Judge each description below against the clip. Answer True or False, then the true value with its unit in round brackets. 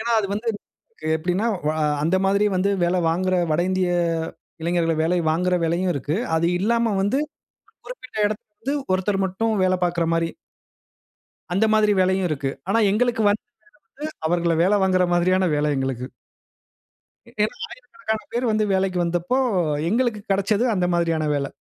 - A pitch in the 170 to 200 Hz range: True (185 Hz)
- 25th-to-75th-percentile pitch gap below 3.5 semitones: False (3.8 semitones)